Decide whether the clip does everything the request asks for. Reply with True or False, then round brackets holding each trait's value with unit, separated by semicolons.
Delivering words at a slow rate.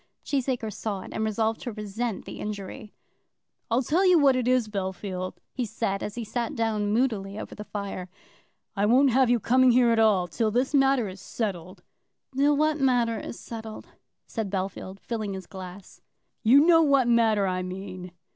False (180 wpm)